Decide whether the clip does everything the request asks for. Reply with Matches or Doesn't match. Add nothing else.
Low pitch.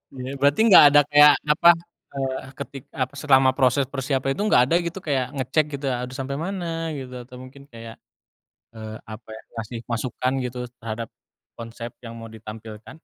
Matches